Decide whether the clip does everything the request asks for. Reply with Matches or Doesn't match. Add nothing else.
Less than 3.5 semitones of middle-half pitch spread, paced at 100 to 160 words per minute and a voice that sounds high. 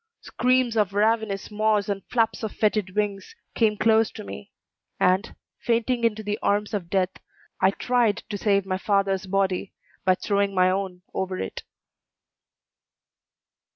Matches